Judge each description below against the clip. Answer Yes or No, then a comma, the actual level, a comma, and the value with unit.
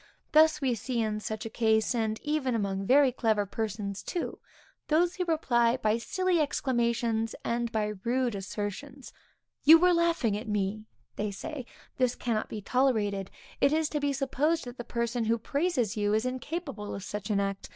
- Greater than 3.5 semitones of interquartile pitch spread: Yes, average, 4.8 semitones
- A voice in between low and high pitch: No, high, 235 Hz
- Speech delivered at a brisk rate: No, average, 175 wpm